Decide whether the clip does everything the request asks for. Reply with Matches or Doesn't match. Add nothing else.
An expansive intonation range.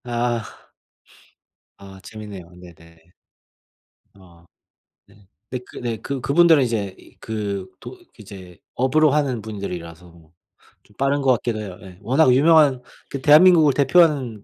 Matches